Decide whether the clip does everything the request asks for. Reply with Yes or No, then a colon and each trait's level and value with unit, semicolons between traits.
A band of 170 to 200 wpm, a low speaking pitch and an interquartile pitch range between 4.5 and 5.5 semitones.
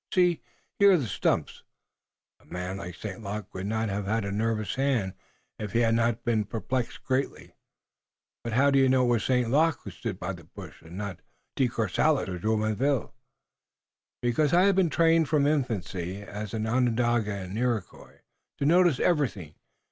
Yes: average, 180 wpm; low, 115 Hz; average, 5.2 semitones